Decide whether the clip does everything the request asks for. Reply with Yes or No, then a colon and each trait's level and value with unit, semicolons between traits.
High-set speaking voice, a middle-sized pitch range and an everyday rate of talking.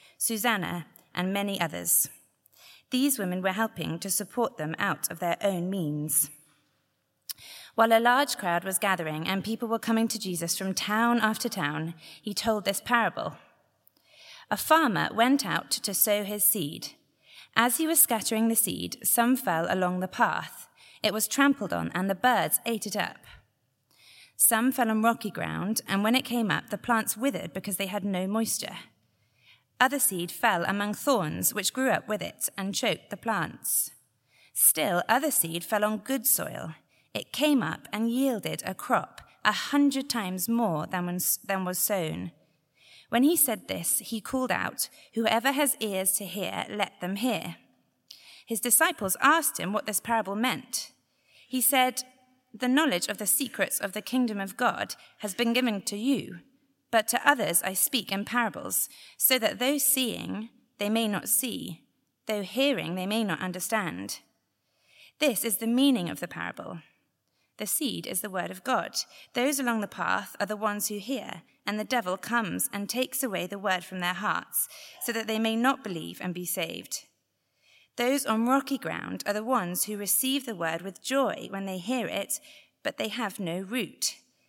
Yes: high, 220 Hz; average, 4.6 semitones; average, 175 wpm